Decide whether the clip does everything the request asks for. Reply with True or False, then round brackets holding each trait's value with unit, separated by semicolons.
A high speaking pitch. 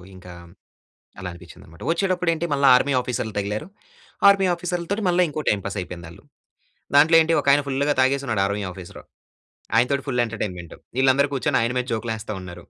False (125 Hz)